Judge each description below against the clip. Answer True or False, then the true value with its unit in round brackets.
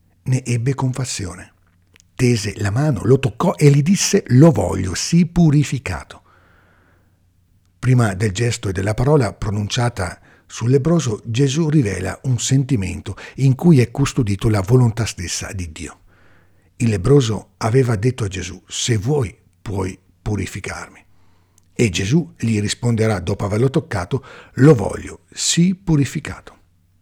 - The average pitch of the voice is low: True (110 Hz)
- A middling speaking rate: True (125 wpm)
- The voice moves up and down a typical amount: False (6.4 semitones)